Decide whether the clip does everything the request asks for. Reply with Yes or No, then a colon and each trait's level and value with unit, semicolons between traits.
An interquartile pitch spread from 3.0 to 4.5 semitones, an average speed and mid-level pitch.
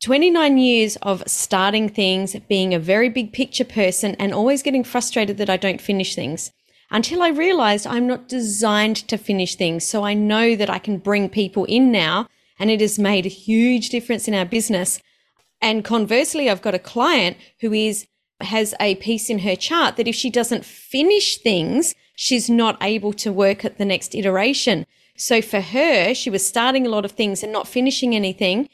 No: average, 3.8 semitones; average, 190 wpm; high, 215 Hz